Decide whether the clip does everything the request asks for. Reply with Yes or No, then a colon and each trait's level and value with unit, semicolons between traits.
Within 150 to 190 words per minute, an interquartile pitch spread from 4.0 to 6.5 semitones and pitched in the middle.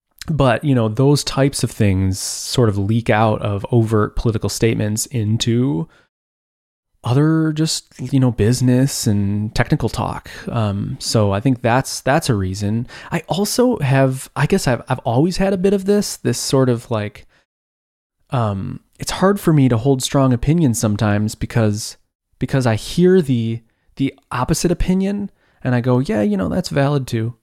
No: average, 165 wpm; average, 4.5 semitones; low, 125 Hz